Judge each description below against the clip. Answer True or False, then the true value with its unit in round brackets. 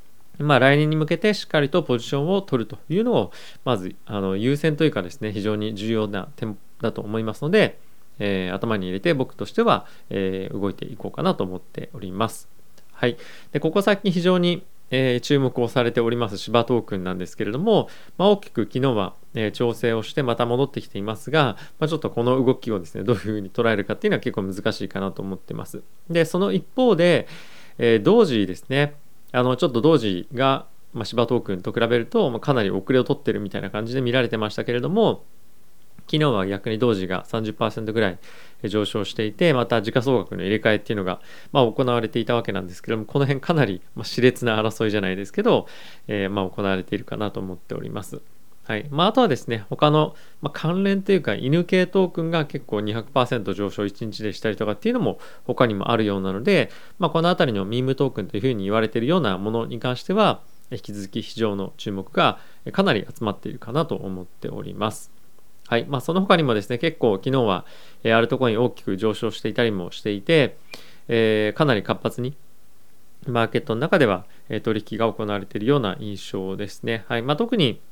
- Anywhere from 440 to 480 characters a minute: False (405 characters per minute)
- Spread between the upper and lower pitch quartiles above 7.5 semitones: False (5.3 semitones)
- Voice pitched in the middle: False (115 Hz)